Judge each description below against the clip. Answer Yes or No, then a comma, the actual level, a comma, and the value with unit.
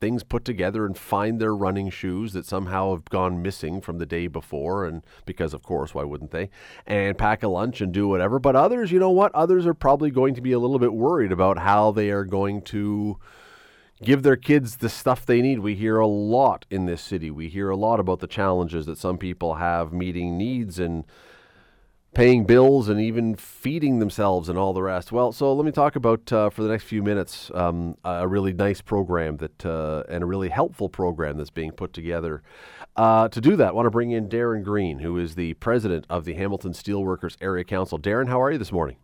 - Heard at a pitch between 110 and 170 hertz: No, low, 100 Hz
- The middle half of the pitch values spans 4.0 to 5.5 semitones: Yes, average, 4.4 semitones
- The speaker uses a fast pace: Yes, fast, 225 wpm